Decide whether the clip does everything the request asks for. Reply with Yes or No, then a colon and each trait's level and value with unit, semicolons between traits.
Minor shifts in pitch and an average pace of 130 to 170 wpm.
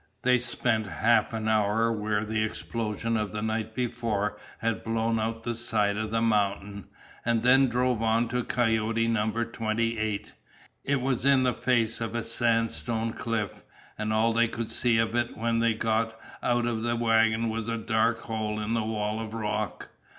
No: narrow, 1.2 semitones; average, 180 wpm